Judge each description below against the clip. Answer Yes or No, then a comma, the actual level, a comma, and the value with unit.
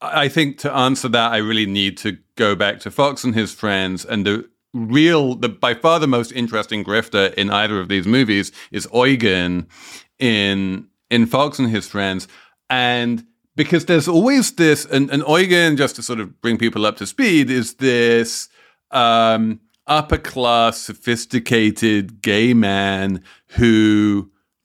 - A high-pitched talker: No, low, 115 Hz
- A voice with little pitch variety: No, average, 3.8 semitones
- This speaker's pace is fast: No, average, 160 wpm